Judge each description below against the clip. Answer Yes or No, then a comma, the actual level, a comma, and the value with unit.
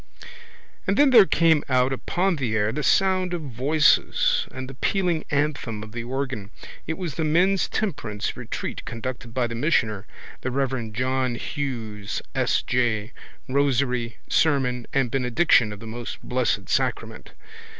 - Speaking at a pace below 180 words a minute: Yes, average, 150 wpm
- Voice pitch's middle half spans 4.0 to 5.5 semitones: Yes, average, 5.2 semitones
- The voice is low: Yes, low, 130 Hz